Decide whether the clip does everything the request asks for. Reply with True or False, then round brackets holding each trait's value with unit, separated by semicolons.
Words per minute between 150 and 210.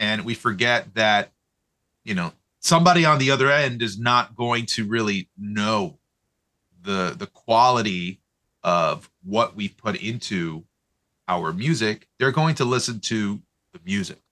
False (140 wpm)